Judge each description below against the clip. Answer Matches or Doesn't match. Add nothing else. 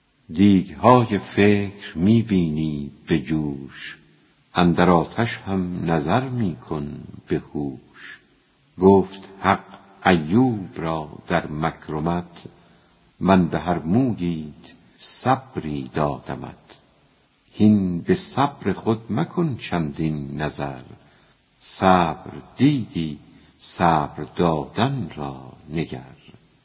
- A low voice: Matches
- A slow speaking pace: Matches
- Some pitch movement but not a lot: Matches